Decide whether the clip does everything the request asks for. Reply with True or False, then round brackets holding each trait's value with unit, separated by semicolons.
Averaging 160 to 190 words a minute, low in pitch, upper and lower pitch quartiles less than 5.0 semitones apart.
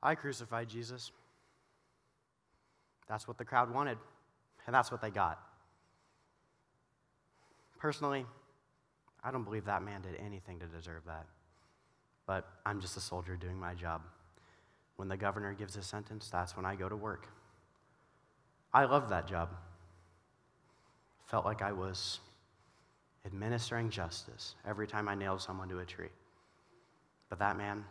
False (140 wpm; 100 Hz; 4.5 semitones)